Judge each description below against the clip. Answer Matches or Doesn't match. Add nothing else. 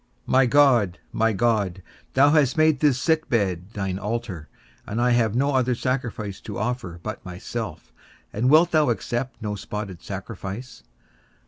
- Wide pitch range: Doesn't match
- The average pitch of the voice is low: Matches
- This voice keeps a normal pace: Matches